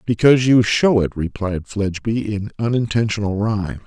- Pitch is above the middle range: No, low, 105 Hz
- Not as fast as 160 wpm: Yes, average, 140 wpm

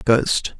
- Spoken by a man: Yes, male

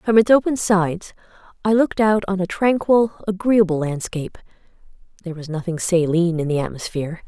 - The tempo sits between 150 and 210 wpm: Yes, average, 155 wpm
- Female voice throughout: Yes, female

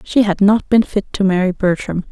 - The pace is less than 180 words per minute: No, fast, 225 wpm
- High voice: Yes, high, 200 Hz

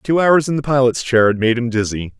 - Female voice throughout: No, male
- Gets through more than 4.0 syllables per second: Yes, 5.6 syllables/s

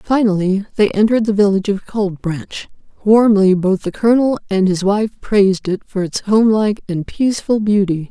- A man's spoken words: No, female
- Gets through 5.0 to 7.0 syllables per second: Yes, 5.4 syllables/s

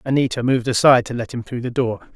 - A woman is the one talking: No, male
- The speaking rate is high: Yes, fast, 250 wpm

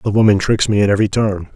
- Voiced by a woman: No, male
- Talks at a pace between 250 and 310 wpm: Yes, fast, 270 wpm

